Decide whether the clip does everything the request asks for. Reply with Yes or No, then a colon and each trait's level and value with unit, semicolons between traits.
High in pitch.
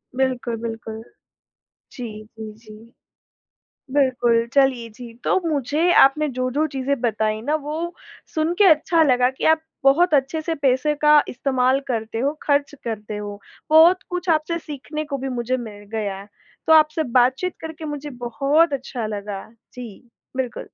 Yes: very high, 265 Hz